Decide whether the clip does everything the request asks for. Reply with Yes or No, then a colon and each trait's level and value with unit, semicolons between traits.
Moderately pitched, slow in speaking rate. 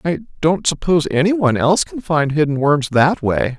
No: medium, 155 Hz; average, 200 wpm